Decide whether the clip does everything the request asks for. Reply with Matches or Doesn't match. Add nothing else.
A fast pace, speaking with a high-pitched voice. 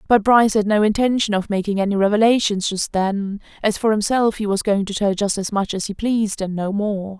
Matches